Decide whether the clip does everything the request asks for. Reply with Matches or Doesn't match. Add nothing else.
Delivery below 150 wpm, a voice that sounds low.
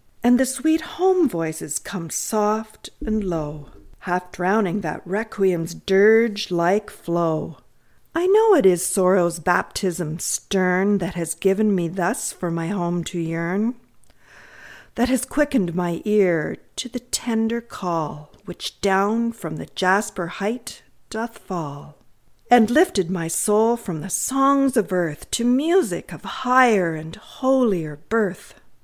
Doesn't match